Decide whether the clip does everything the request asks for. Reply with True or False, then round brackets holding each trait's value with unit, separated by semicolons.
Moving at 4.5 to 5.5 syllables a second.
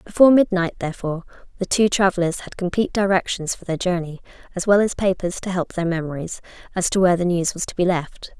False (6.3 syllables/s)